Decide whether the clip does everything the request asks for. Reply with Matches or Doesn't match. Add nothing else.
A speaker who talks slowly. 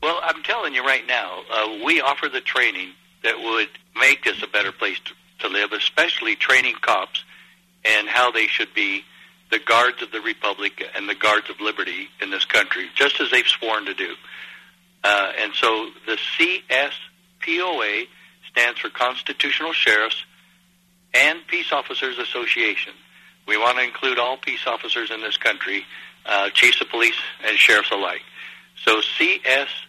Doesn't match